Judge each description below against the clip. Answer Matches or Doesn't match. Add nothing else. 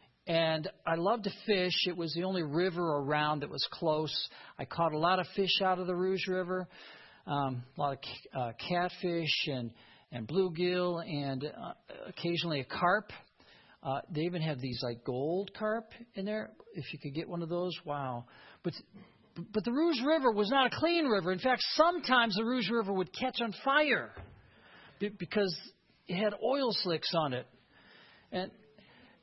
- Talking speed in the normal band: Matches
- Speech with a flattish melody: Doesn't match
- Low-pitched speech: Doesn't match